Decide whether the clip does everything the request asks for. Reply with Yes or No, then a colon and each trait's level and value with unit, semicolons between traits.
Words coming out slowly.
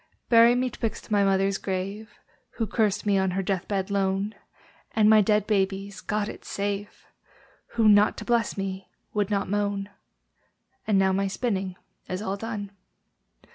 No: average, 160 wpm